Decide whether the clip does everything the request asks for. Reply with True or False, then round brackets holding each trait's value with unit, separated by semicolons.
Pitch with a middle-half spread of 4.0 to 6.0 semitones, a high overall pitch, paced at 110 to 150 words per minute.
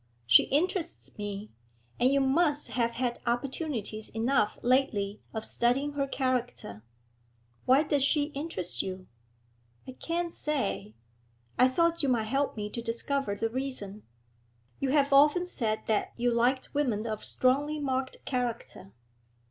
True (4.4 semitones; 255 Hz; 140 wpm)